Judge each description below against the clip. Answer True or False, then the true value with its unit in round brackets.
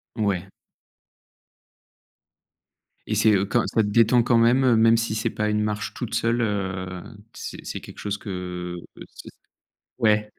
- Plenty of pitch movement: False (2.8 semitones)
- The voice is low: True (105 Hz)